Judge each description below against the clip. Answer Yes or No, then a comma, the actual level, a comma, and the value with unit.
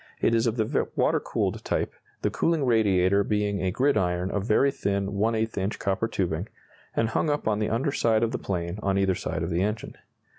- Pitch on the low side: Yes, low, 105 Hz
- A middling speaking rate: No, fast, 210 wpm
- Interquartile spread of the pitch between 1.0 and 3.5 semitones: Yes, average, 2.9 semitones